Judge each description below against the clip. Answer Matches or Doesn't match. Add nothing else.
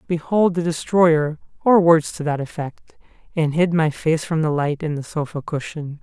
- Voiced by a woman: Doesn't match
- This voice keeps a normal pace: Matches